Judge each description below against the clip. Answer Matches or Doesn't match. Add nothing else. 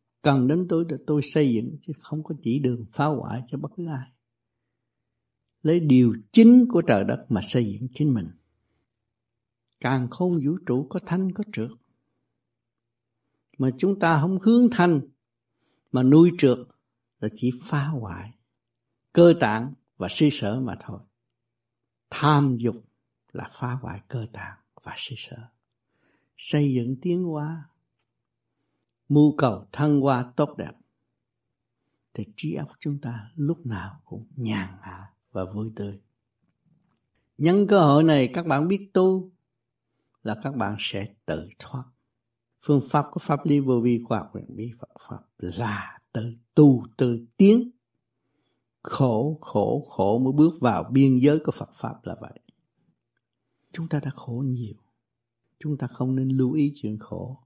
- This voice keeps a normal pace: Doesn't match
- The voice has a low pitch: Matches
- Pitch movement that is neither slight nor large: Matches